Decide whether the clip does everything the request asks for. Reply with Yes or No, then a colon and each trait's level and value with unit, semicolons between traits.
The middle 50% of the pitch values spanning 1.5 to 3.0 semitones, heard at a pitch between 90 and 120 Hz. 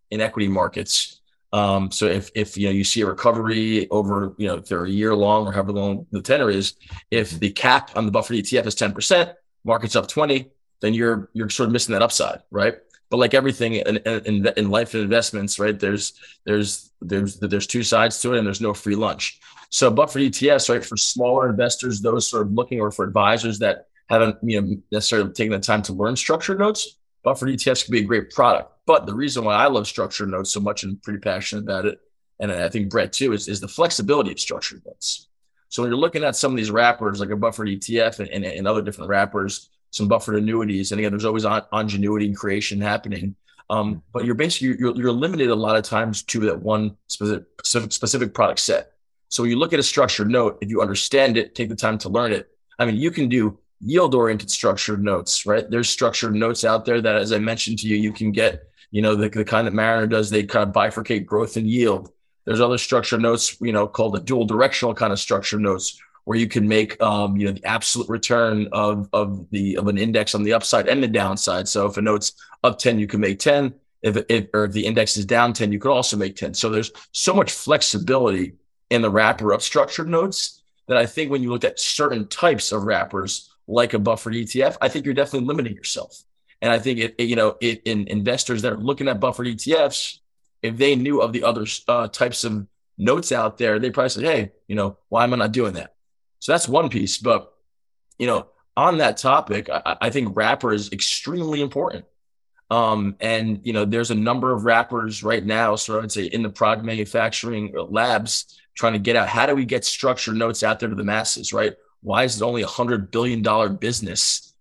Yes: narrow, 2.4 semitones; low, 110 Hz